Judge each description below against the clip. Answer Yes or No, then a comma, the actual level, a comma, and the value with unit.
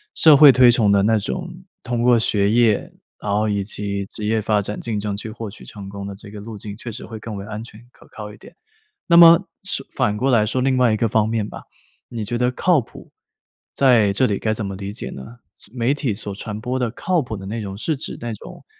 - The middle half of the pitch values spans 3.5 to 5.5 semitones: No, average, 2.9 semitones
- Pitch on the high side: No, low, 110 Hz